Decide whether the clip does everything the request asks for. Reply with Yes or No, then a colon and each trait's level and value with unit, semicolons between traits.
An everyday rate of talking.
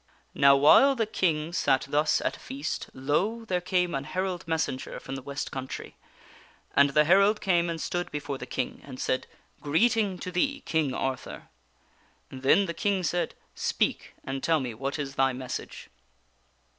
Yes: average, 170 wpm